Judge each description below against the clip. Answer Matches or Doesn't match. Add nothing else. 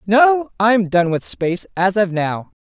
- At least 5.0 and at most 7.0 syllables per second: Doesn't match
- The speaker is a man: Doesn't match